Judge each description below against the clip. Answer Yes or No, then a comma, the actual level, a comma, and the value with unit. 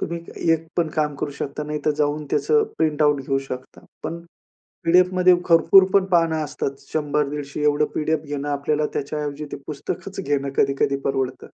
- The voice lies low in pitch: No, medium, 150 Hz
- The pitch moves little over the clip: Yes, narrow, 2.3 semitones